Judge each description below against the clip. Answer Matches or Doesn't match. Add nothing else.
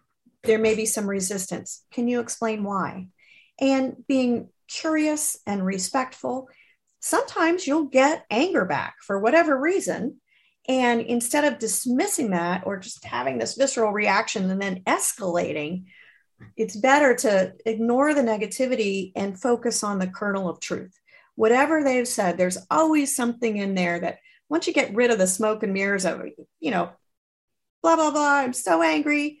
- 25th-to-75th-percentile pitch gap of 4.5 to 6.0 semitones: Matches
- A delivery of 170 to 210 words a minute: Doesn't match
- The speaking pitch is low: Doesn't match